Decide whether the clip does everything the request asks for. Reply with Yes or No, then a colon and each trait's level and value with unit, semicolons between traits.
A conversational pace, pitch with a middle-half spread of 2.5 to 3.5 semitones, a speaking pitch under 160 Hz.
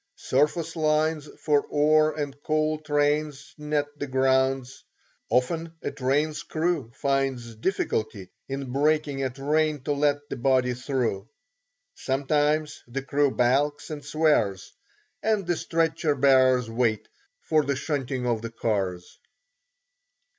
No: slow, 125 wpm; average, 3.0 semitones; medium, 140 Hz